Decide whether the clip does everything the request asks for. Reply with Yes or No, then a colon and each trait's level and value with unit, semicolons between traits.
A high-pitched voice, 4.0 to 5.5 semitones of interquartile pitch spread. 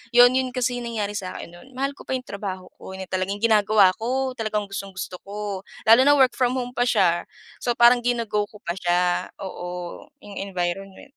Yes: high, 210 Hz; average, 4.5 semitones